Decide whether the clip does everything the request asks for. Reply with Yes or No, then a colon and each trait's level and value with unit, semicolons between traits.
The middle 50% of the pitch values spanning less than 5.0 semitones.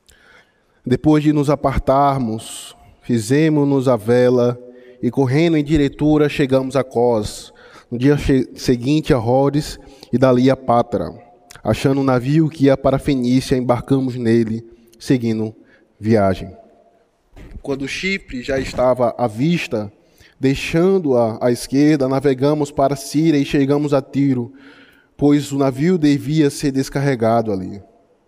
Yes: average, 3.0 semitones